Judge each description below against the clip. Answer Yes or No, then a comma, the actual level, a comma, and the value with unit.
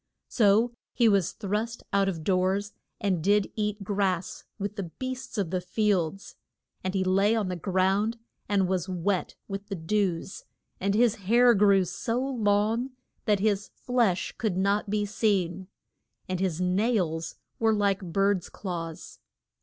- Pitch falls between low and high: No, high, 200 Hz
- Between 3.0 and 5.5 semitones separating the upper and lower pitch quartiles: No, narrow, 2.4 semitones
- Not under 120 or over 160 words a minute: Yes, average, 150 wpm